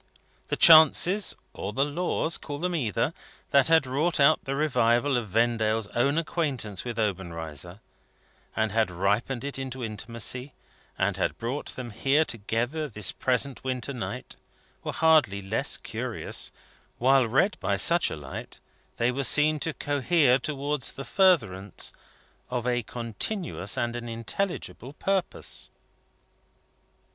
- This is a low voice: Yes, low, 125 Hz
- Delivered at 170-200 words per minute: No, slow, 135 wpm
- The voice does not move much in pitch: No, average, 4.8 semitones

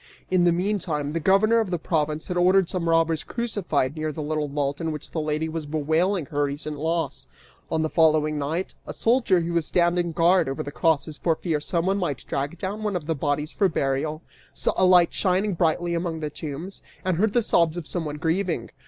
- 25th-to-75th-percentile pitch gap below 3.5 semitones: Yes, average, 2.9 semitones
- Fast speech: Yes, fast, 210 wpm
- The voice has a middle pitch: Yes, medium, 165 Hz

